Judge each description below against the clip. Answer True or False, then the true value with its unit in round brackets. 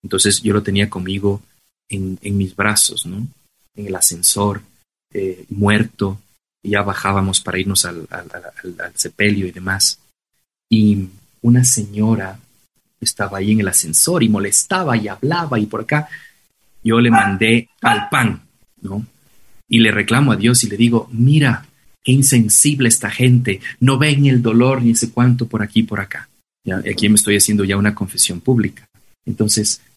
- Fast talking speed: False (160 wpm)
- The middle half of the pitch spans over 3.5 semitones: False (3.0 semitones)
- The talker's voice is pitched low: True (105 Hz)